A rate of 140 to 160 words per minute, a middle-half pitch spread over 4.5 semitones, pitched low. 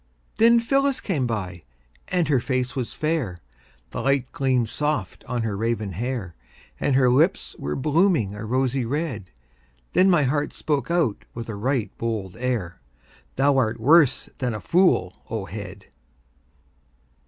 Yes: average, 150 wpm; wide, 5.4 semitones; low, 125 Hz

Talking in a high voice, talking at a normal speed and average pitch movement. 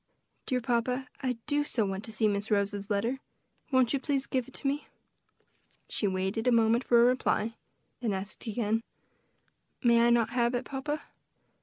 Yes: high, 235 Hz; average, 175 wpm; average, 3.2 semitones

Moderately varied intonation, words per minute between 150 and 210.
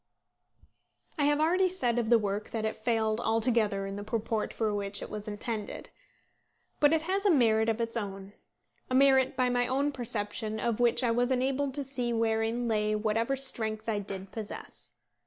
Yes: average, 3.3 semitones; average, 185 wpm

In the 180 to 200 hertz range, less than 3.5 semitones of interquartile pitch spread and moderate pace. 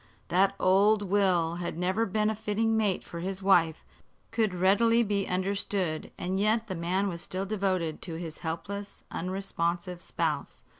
Yes: high, 190 Hz; average, 2.9 semitones; average, 155 wpm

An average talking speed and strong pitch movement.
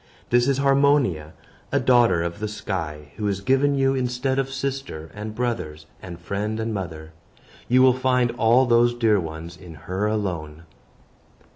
Yes: average, 160 wpm; wide, 7.0 semitones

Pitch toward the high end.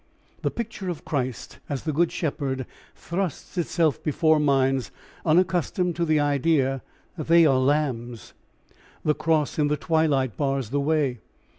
No: medium, 150 Hz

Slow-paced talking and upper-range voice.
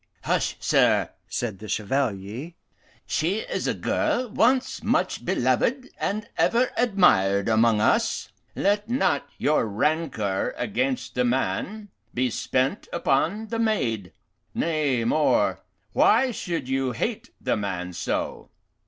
No: slow, 120 wpm; medium, 140 Hz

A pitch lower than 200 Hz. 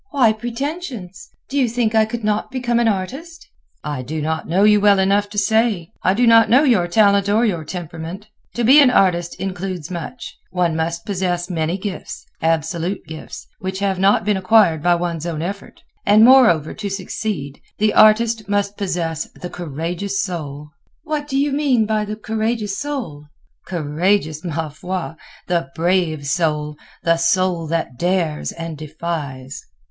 Yes: high, 190 Hz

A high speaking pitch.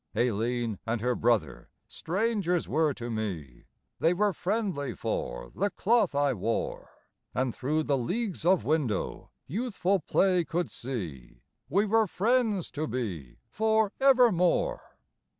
No: medium, 155 Hz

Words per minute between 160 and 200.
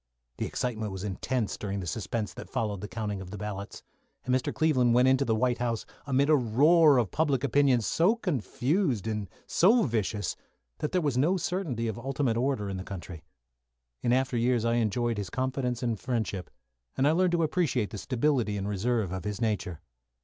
Yes: average, 195 wpm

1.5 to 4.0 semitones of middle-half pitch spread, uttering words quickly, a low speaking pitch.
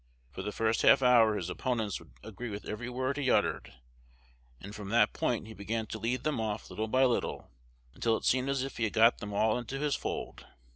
Yes: average, 3.1 semitones; fast, 225 wpm; low, 115 Hz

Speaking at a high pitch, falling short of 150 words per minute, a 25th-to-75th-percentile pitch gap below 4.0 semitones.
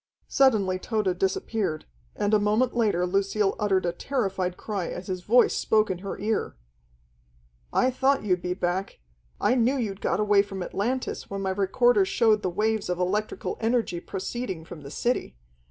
No: high, 200 Hz; average, 170 wpm; average, 3.3 semitones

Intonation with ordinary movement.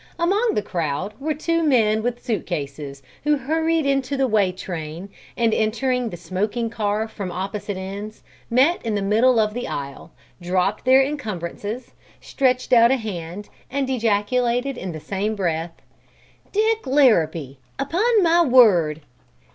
No: wide, 6.0 semitones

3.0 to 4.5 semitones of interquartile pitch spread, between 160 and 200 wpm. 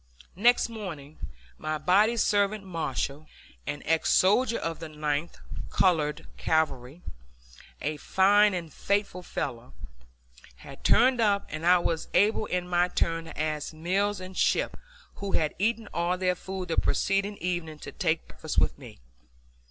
No: average, 4.2 semitones; average, 145 wpm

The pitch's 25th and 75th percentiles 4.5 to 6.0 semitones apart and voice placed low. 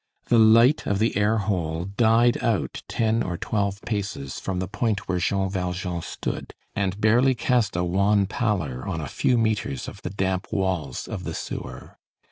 No: average, 3.5 semitones; low, 100 Hz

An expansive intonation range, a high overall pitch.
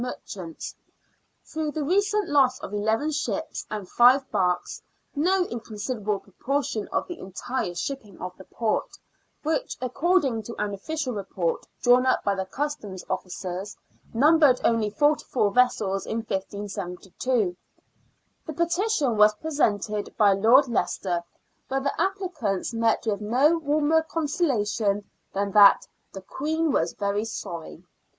Yes: wide, 6.6 semitones; high, 230 Hz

